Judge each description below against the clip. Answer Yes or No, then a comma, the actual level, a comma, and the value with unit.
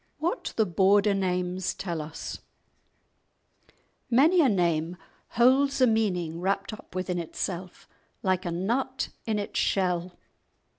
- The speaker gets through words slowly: Yes, slow, 120 wpm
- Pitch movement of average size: Yes, average, 4.0 semitones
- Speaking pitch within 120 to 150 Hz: No, high, 190 Hz